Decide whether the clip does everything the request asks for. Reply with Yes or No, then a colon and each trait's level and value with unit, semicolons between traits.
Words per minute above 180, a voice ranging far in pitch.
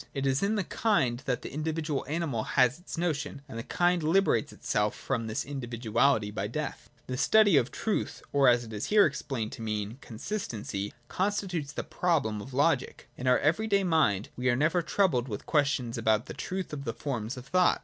Yes: average, 200 wpm; wide, 6.2 semitones